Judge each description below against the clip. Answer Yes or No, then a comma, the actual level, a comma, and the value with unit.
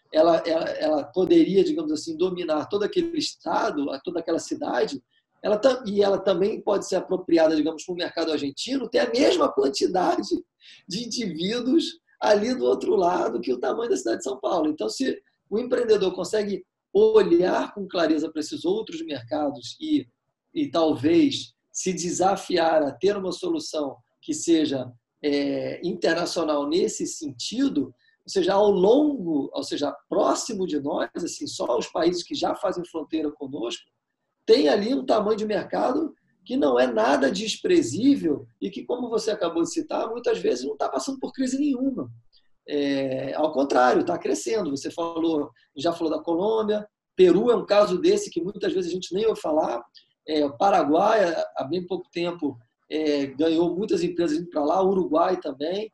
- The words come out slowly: No, average, 165 wpm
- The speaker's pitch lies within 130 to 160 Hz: No, high, 205 Hz